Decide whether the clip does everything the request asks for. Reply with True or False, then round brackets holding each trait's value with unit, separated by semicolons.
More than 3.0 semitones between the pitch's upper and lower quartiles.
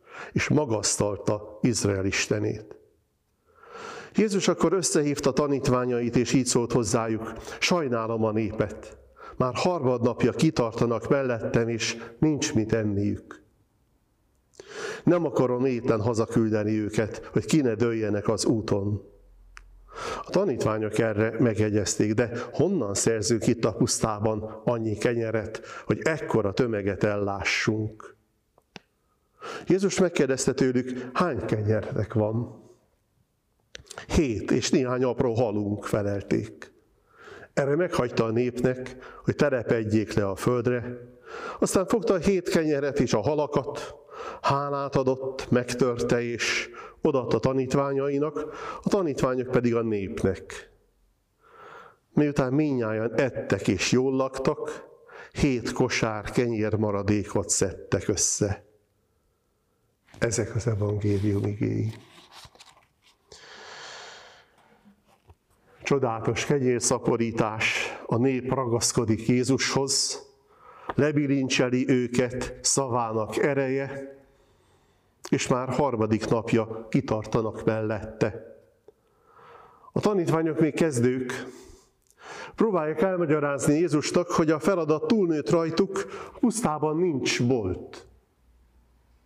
True (5.3 semitones)